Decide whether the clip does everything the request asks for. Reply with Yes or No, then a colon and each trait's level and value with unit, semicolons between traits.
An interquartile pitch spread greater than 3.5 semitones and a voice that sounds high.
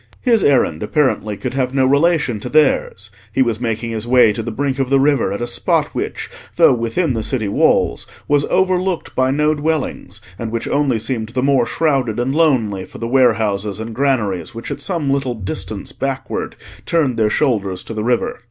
No: average, 4.3 semitones; low, 125 Hz